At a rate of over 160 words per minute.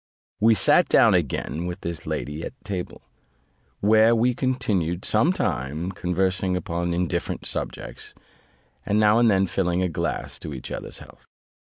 No: average, 150 wpm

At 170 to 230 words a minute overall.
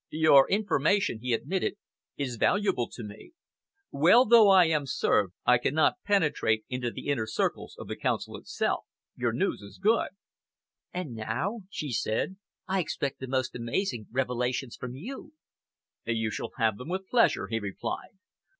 No: average, 155 wpm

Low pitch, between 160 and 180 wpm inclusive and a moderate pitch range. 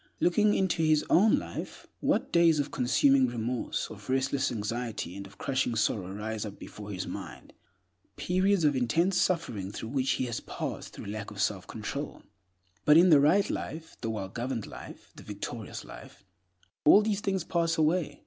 No: low, 130 Hz; average, 170 wpm; wide, 7.5 semitones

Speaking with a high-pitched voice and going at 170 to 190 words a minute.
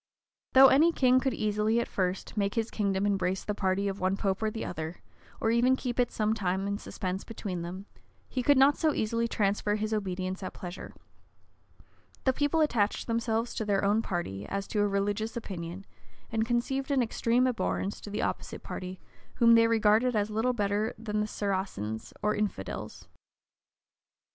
Yes: high, 210 Hz; average, 175 wpm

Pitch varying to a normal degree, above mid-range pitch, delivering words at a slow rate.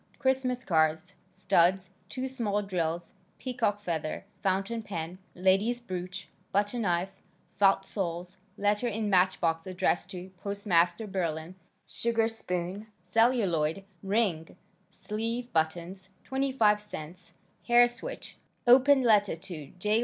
Yes: average, 4.3 semitones; high, 195 Hz; slow, 110 wpm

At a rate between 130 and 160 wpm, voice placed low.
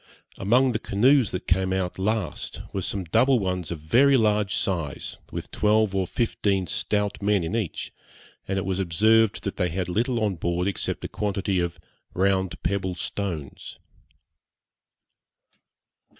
Yes: average, 150 wpm; low, 100 Hz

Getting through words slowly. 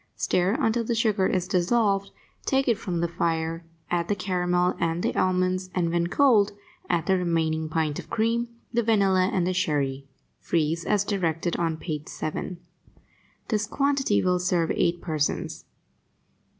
No: average, 155 wpm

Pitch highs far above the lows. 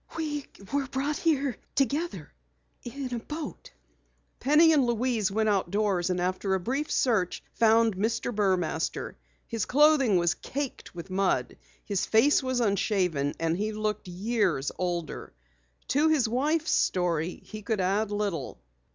Yes: wide, 6.3 semitones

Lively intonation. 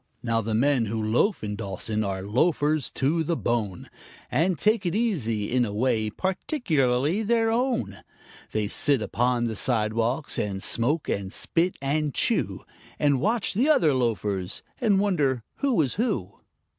Yes: wide, 8.4 semitones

